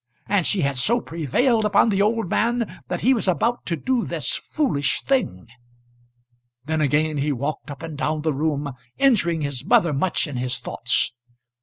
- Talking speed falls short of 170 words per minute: No, average, 175 wpm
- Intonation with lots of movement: Yes, wide, 7.7 semitones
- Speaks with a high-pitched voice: No, medium, 165 Hz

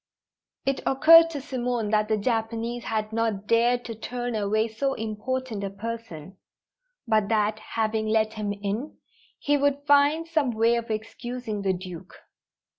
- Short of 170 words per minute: Yes, average, 150 wpm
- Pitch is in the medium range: No, high, 225 Hz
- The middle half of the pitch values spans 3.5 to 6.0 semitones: No, average, 2.8 semitones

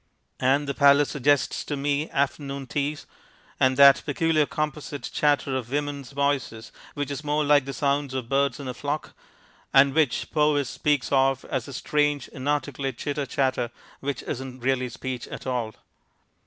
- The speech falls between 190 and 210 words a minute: No, average, 160 wpm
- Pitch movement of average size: No, narrow, 1.7 semitones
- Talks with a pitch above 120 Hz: Yes, medium, 140 Hz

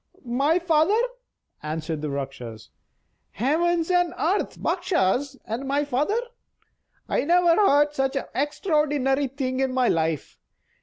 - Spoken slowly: Yes, slow, 120 wpm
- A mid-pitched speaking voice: No, very high, 275 Hz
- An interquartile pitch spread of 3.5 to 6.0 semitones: Yes, wide, 5.4 semitones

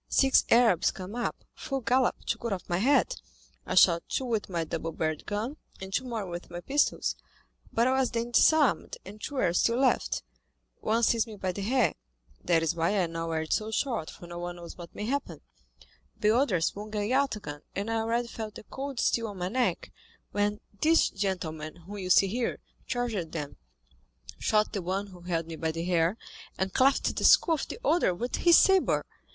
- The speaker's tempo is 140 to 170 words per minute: No, fast, 205 wpm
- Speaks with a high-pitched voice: Yes, high, 205 Hz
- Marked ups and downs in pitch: Yes, wide, 5.8 semitones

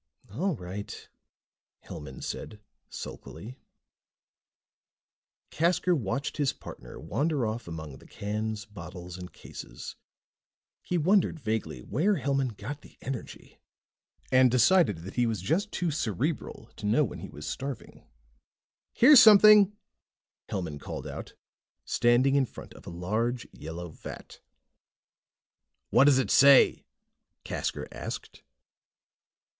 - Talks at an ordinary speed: No, slow, 120 wpm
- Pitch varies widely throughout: Yes, wide, 7.3 semitones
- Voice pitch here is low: Yes, low, 120 Hz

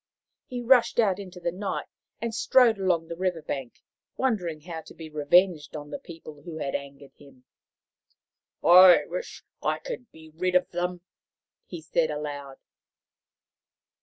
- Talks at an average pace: Yes, average, 155 wpm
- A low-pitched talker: No, medium, 170 Hz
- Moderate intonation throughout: Yes, average, 3.9 semitones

